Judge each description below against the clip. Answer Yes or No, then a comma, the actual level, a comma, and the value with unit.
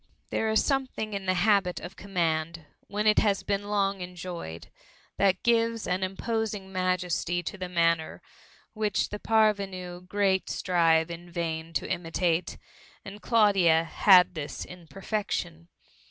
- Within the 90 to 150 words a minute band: Yes, average, 140 wpm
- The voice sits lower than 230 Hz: Yes, medium, 185 Hz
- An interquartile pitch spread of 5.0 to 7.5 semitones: No, average, 3.2 semitones